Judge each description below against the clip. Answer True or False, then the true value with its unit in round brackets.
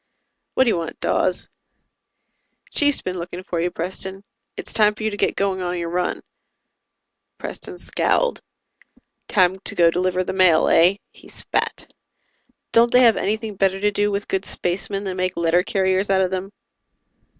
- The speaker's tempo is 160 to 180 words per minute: True (170 wpm)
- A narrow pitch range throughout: True (2.3 semitones)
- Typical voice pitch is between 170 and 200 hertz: True (190 Hz)